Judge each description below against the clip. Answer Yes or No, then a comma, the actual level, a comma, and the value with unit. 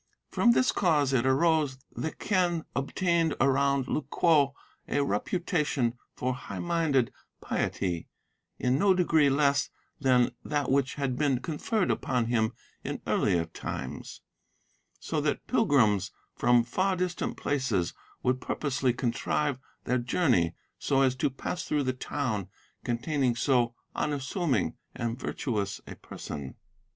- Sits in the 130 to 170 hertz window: Yes, low, 135 Hz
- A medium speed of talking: No, slow, 130 wpm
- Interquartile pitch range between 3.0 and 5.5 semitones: Yes, average, 3.9 semitones